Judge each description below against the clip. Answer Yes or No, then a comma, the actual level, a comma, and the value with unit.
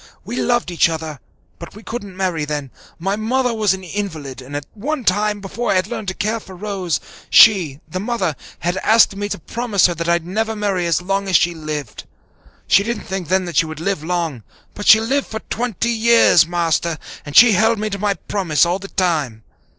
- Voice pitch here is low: No, high, 190 Hz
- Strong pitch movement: No, average, 4.3 semitones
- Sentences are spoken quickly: Yes, fast, 210 wpm